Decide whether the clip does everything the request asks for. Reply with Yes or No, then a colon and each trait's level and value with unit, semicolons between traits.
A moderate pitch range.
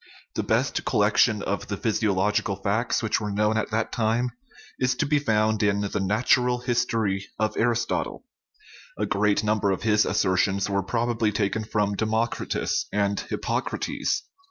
No: narrow, 2.3 semitones